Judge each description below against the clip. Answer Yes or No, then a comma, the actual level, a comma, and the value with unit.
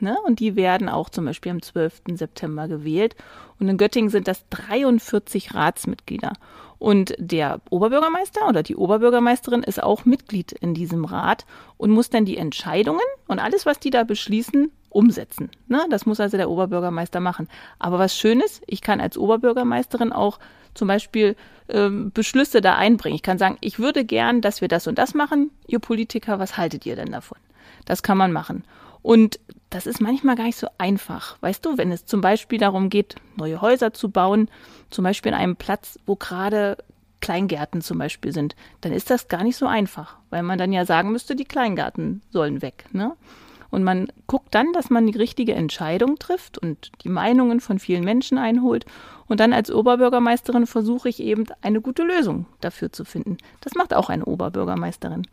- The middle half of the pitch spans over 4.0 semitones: Yes, average, 4.5 semitones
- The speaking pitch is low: No, high, 215 Hz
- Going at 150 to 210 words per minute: Yes, average, 180 wpm